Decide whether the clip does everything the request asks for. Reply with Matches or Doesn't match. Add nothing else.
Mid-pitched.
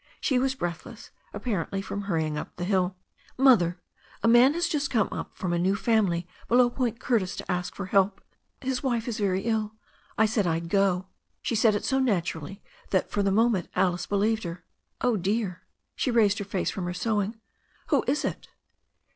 Doesn't match